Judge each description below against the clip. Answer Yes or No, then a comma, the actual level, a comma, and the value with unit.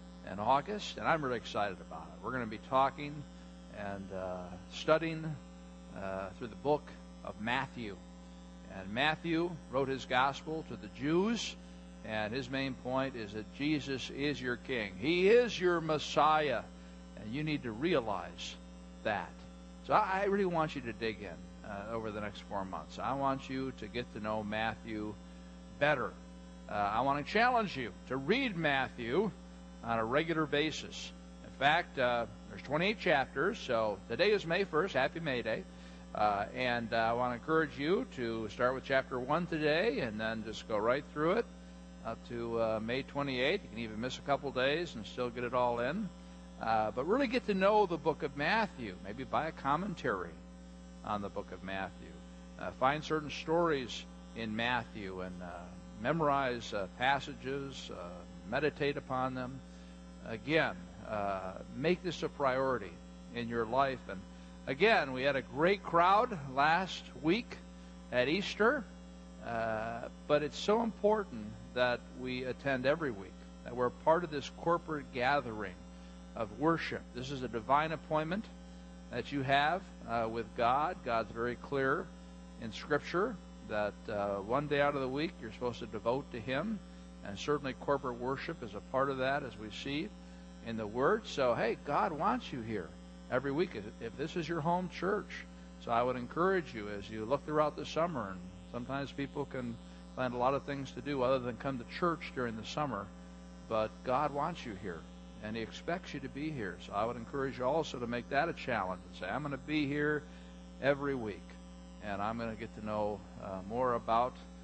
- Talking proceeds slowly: No, average, 180 wpm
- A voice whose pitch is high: No, low, 120 Hz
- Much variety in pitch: Yes, wide, 8.0 semitones